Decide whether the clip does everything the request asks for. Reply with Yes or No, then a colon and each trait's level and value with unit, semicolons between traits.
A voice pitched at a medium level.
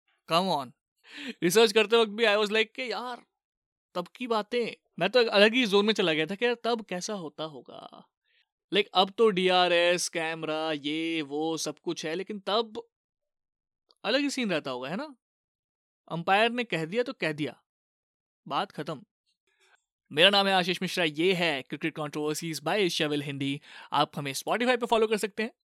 No: high, 195 Hz